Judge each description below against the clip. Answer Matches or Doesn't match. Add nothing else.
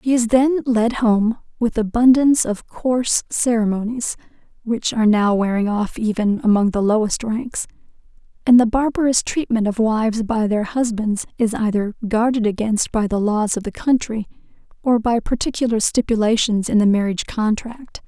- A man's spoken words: Doesn't match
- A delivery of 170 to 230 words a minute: Doesn't match